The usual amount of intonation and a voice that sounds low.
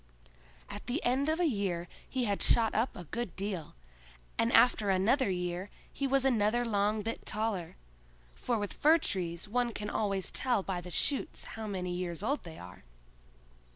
No: average, 4.8 semitones; high, 210 Hz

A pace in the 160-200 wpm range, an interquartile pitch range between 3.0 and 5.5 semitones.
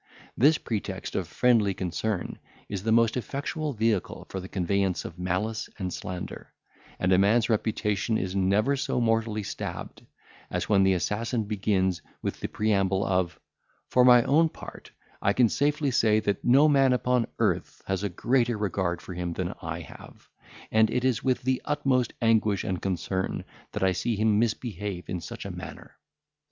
Yes: average, 170 wpm; average, 4.2 semitones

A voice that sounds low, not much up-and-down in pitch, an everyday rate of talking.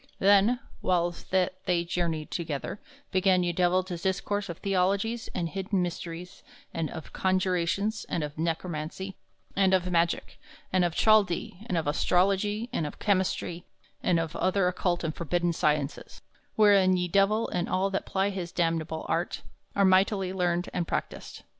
No: medium, 180 Hz; narrow, 2.3 semitones; average, 155 wpm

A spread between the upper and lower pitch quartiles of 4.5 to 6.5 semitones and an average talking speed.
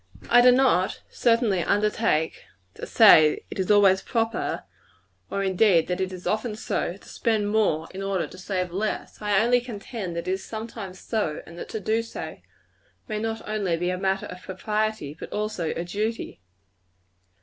No: average, 3.2 semitones; average, 180 wpm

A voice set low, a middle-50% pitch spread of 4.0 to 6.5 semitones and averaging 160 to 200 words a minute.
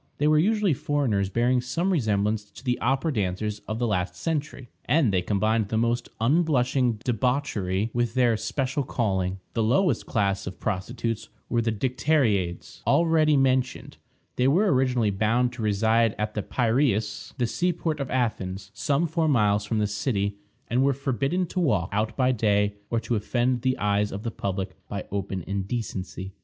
Yes: low, 115 Hz; average, 4.6 semitones; average, 170 wpm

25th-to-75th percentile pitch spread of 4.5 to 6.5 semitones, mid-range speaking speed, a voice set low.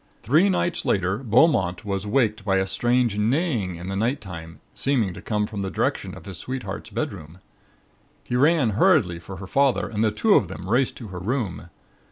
Yes: average, 5.2 semitones; average, 190 wpm; low, 105 Hz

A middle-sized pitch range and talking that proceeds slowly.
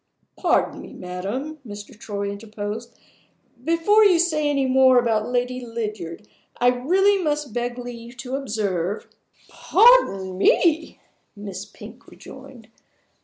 No: wide, 5.8 semitones; slow, 120 wpm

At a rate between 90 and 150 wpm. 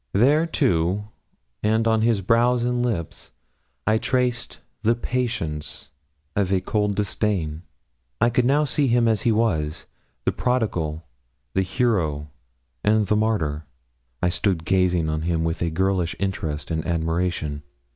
Yes: average, 140 wpm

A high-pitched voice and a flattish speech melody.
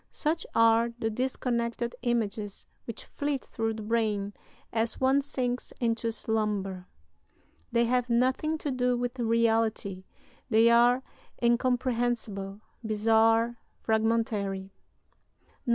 Yes: high, 230 Hz; narrow, 1.9 semitones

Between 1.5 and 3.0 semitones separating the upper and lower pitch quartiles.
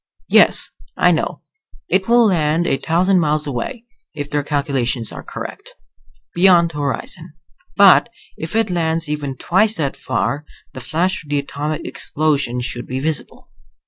No: average, 3.5 semitones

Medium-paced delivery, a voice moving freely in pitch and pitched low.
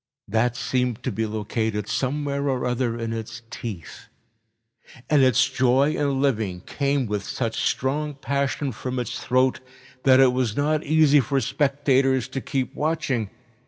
No: average, 150 wpm; average, 3.4 semitones; low, 130 Hz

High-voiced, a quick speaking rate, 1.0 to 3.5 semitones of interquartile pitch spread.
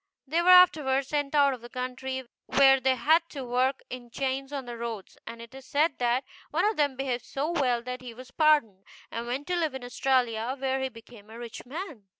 Yes: very high, 260 Hz; fast, 220 wpm; average, 2.8 semitones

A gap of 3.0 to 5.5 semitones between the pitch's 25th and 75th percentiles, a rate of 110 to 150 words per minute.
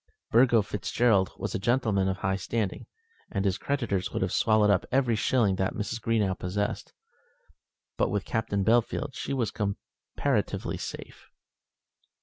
Yes: average, 3.3 semitones; average, 140 wpm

